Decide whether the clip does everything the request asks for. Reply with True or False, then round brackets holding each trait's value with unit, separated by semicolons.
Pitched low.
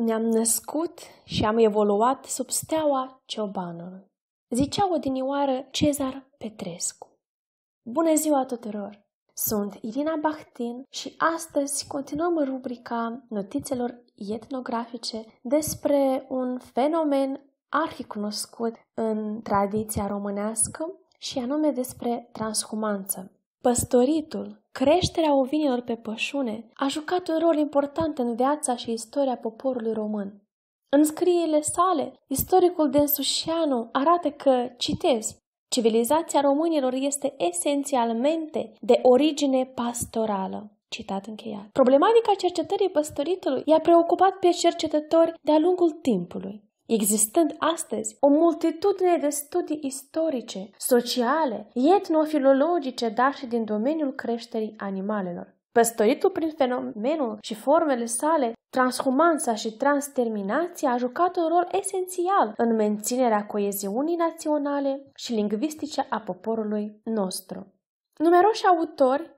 False (265 Hz)